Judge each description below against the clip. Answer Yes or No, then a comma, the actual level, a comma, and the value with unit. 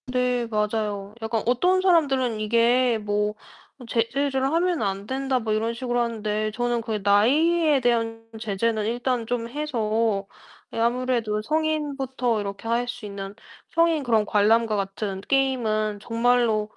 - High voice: Yes, high, 230 Hz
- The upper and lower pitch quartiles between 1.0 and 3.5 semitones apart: Yes, average, 3.2 semitones